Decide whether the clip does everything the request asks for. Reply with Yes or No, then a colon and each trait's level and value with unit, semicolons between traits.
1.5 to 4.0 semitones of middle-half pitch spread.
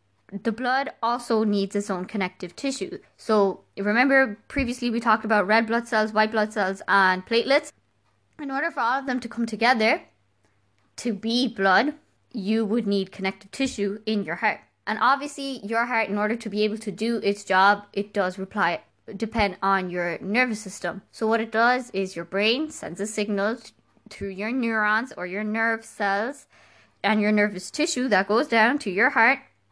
Yes: average, 2.8 semitones